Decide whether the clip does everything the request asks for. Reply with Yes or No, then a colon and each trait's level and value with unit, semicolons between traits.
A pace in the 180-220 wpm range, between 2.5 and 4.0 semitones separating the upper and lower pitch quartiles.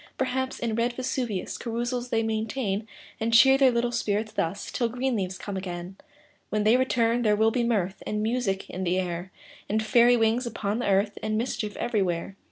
Yes: average, 185 wpm; average, 3.3 semitones